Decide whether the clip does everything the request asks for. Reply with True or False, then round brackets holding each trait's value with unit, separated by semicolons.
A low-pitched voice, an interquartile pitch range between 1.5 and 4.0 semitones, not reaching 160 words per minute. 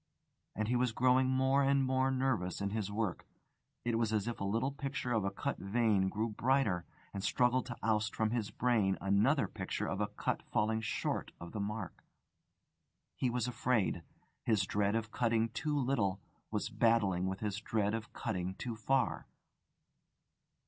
False (110 Hz; 3.6 semitones; 170 wpm)